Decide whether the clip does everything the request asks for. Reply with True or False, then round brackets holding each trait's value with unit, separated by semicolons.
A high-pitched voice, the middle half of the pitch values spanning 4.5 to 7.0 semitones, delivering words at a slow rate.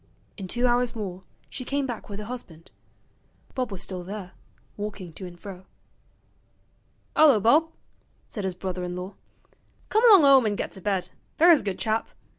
False (210 Hz; 5.1 semitones; 175 wpm)